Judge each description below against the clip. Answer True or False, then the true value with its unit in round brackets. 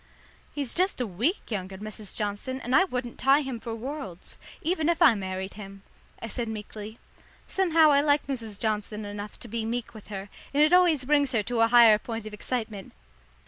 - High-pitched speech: True (230 Hz)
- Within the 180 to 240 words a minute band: True (195 wpm)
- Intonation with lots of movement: False (5.0 semitones)